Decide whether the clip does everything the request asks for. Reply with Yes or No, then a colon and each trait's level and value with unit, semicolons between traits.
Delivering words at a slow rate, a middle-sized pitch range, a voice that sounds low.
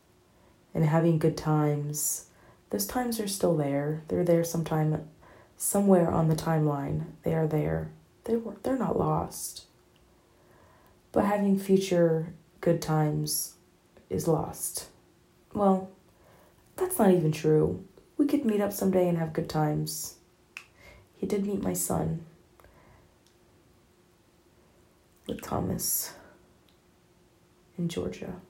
No: slow, 115 wpm; average, 4.1 semitones; medium, 165 Hz